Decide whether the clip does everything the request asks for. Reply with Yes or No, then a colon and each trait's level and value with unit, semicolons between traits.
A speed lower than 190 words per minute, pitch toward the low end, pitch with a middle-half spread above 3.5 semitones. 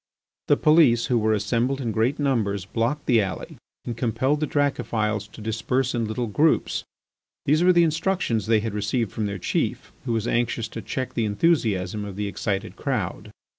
Yes: average, 180 wpm; low, 115 Hz; average, 4.1 semitones